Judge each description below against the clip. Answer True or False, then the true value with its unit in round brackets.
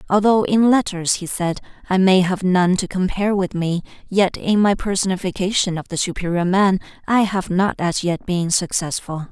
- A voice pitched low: False (185 Hz)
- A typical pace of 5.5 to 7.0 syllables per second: False (5.0 syllables/s)